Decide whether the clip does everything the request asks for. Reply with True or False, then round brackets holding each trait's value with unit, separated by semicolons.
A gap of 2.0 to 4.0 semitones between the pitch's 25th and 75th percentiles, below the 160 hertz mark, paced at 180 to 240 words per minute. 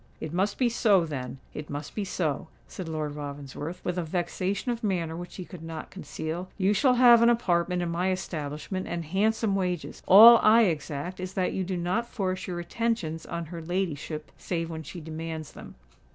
False (3.4 semitones; 175 Hz; 185 wpm)